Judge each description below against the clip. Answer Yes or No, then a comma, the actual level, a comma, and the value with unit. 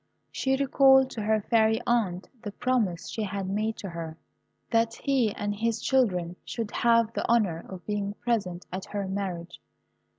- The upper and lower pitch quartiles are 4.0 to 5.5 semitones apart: No, average, 3.6 semitones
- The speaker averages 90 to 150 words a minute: No, average, 165 wpm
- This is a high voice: Yes, high, 210 Hz